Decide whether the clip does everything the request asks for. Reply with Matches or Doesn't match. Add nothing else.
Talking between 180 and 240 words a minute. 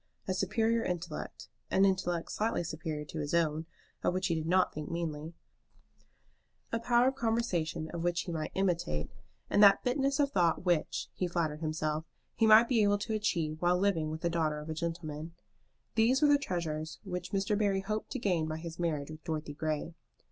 Matches